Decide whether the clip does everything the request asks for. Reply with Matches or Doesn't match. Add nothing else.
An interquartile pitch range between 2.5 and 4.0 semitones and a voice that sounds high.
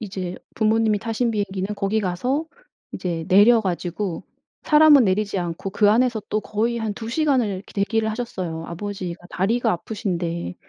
Matches